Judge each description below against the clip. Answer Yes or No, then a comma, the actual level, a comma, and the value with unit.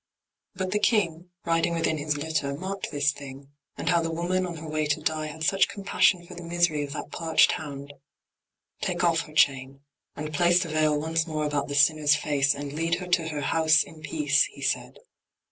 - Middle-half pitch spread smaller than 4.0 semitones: Yes, narrow, 2.6 semitones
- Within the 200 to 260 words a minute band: Yes, fast, 205 wpm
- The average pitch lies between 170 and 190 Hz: No, medium, 155 Hz